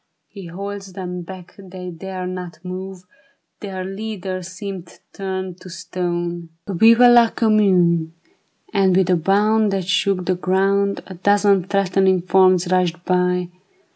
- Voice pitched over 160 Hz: Yes, medium, 185 Hz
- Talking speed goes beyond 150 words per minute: No, average, 140 wpm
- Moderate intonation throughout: No, narrow, 1.6 semitones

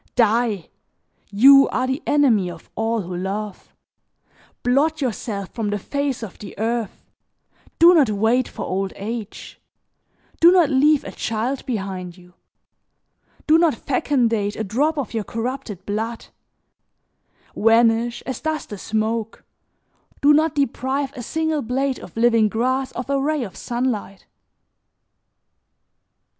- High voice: Yes, high, 235 Hz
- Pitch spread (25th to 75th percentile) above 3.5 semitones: Yes, average, 4.5 semitones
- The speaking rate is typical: No, slow, 130 wpm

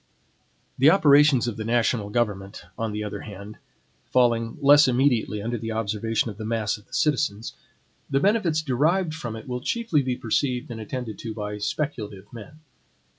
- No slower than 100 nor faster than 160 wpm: No, average, 170 wpm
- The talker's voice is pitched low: Yes, low, 120 Hz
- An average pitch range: Yes, average, 4.8 semitones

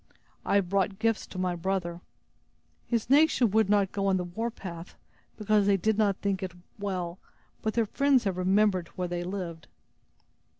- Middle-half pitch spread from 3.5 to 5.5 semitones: No, average, 2.9 semitones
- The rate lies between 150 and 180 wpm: Yes, average, 170 wpm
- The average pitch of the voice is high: Yes, high, 195 Hz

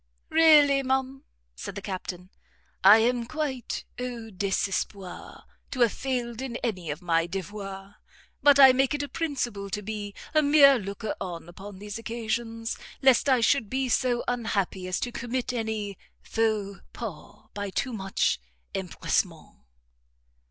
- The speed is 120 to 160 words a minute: Yes, average, 145 wpm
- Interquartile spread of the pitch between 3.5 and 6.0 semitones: Yes, average, 4.6 semitones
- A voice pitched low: No, high, 225 Hz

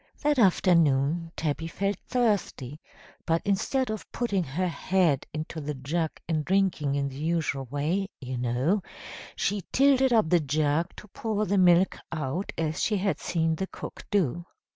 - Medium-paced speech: Yes, average, 160 wpm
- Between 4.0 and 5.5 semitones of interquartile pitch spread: Yes, average, 5.0 semitones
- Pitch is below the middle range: No, medium, 170 Hz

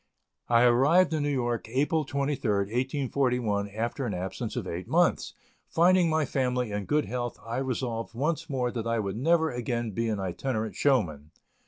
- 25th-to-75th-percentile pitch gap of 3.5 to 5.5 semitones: Yes, average, 4.1 semitones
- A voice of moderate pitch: No, low, 125 Hz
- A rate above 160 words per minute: Yes, average, 170 wpm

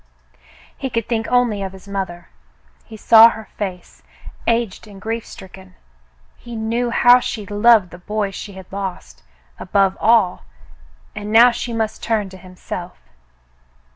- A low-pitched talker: No, high, 210 Hz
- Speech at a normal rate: Yes, average, 145 wpm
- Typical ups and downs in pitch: Yes, average, 3.2 semitones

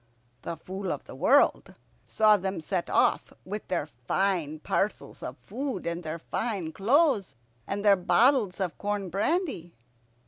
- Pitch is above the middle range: Yes, high, 195 Hz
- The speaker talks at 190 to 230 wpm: No, average, 145 wpm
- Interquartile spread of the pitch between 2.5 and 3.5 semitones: No, average, 4.0 semitones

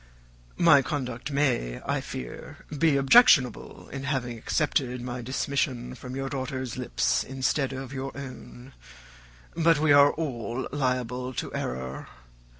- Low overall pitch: Yes, low, 130 Hz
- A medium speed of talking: No, slow, 130 wpm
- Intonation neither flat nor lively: No, narrow, 2.2 semitones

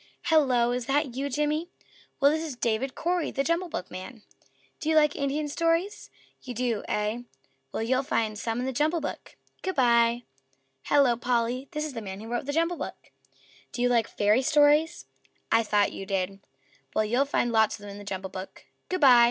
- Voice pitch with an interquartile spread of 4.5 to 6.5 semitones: Yes, average, 5.0 semitones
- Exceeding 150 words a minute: Yes, average, 195 wpm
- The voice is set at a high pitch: Yes, very high, 250 Hz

